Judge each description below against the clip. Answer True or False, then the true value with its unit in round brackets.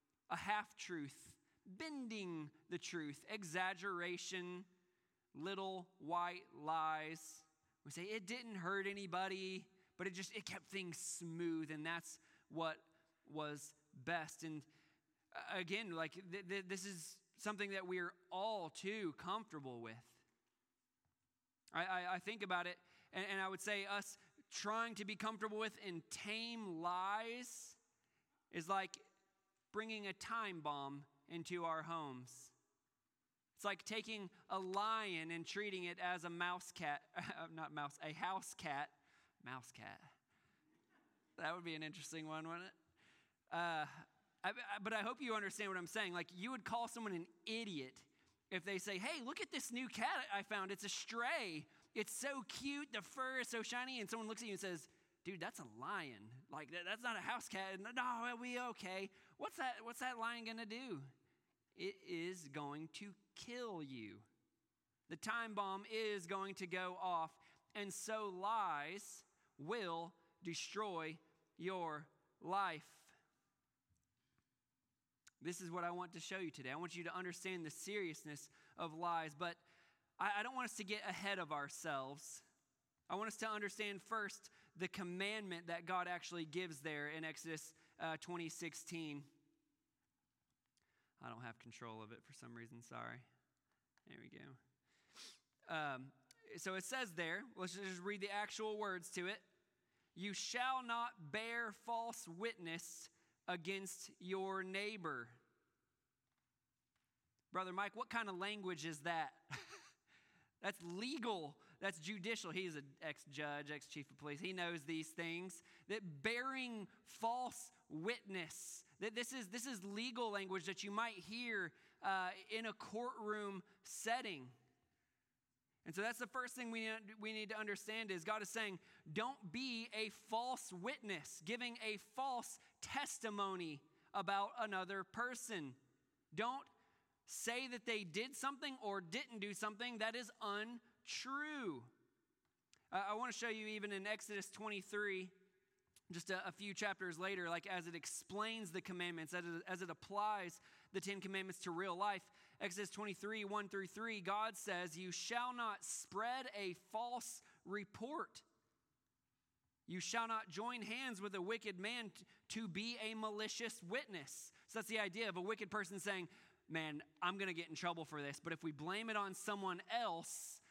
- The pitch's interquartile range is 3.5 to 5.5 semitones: True (4.4 semitones)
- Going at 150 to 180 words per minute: True (155 wpm)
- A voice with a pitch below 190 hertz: False (195 Hz)